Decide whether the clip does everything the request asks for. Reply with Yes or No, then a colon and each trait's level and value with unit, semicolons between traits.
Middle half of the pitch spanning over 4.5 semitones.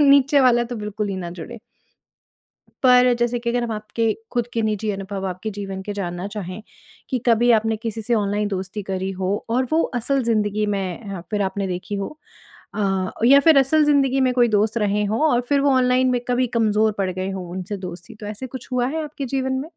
No: average, 4.2 semitones